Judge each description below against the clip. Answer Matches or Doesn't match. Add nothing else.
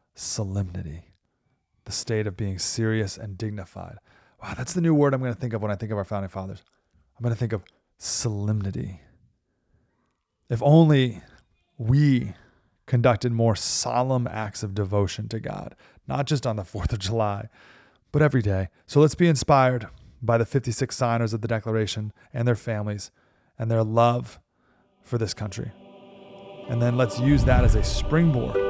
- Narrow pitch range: Doesn't match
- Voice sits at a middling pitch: Doesn't match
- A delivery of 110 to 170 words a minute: Matches